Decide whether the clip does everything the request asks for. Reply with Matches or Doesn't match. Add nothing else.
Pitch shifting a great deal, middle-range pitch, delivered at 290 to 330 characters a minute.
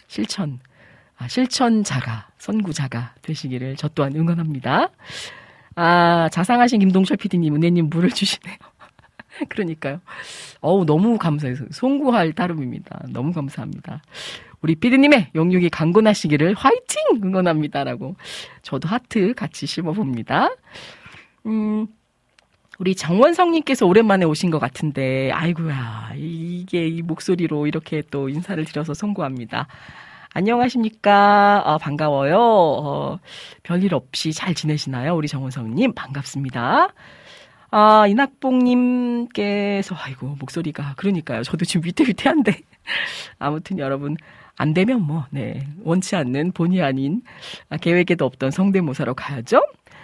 Matches